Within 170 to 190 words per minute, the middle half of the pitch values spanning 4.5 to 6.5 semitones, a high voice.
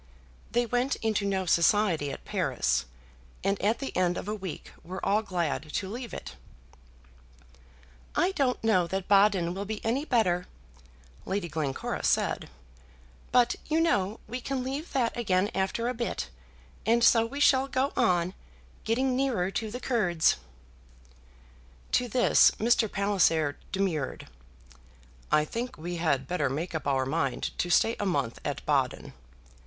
No: average, 150 wpm; wide, 5.5 semitones; high, 200 Hz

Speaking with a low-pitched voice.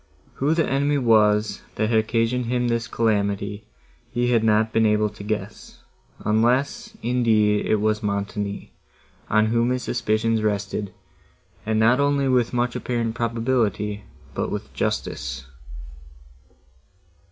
Yes: low, 110 Hz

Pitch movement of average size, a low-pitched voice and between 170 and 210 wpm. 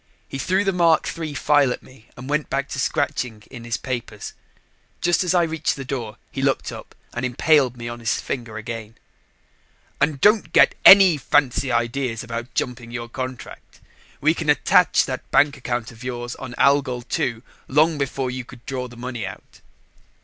Yes: average, 3.5 semitones; low, 130 Hz; average, 180 wpm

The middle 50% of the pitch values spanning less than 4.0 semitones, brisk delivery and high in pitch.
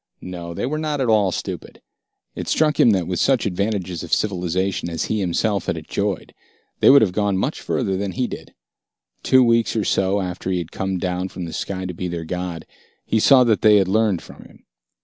No: average, 3.5 semitones; fast, 215 wpm; very low, 95 Hz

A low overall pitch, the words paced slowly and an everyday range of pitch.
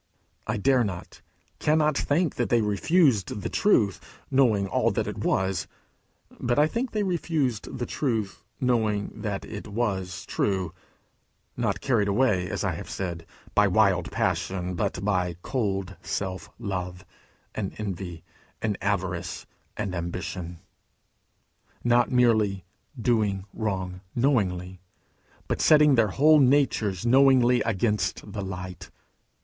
Yes: low, 105 Hz; slow, 125 wpm; average, 4.8 semitones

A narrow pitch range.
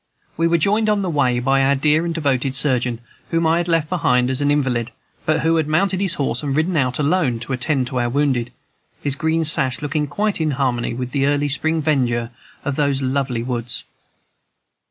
No: average, 3.9 semitones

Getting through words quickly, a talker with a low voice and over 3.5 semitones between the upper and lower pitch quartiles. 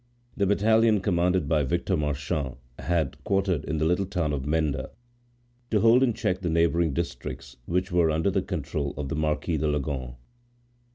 No: average, 170 wpm; very low, 85 Hz; average, 4.1 semitones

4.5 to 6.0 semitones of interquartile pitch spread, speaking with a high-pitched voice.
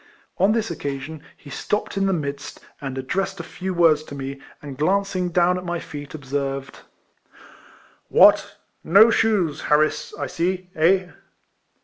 No: average, 4.9 semitones; medium, 165 Hz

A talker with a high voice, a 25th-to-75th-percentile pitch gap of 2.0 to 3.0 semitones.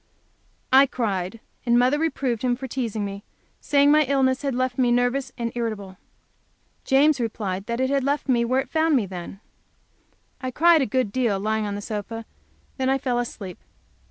No: high, 245 Hz; average, 3.8 semitones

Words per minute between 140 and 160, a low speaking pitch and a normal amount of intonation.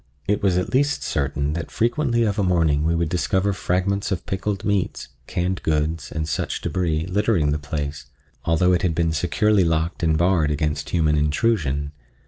No: average, 175 wpm; very low, 85 Hz; average, 4.0 semitones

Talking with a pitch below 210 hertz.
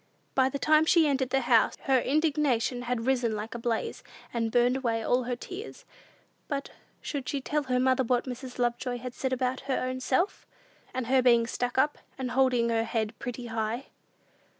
No: very high, 255 Hz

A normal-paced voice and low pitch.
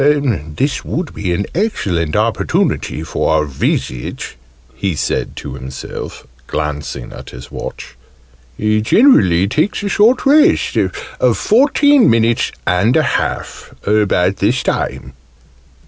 No: slow, 120 wpm; low, 105 Hz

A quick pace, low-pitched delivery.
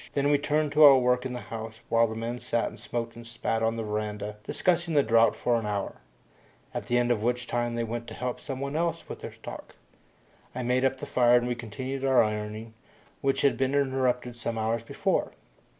Yes: fast, 220 wpm; low, 120 Hz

